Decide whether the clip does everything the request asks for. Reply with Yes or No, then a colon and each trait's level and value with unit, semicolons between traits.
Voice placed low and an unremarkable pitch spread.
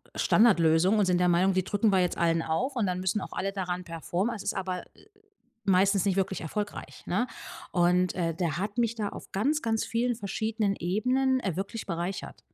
No: high, 195 Hz; average, 3.4 semitones